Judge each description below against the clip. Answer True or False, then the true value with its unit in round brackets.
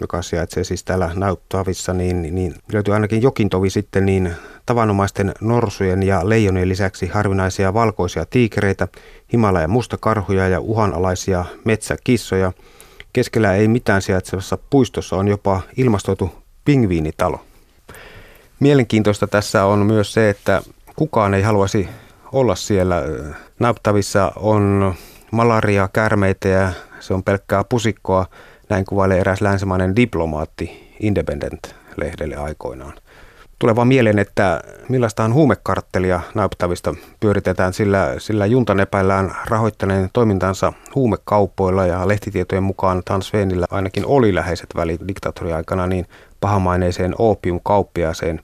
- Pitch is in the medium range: False (100 Hz)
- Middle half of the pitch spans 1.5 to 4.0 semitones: True (2.7 semitones)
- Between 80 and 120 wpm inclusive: True (110 wpm)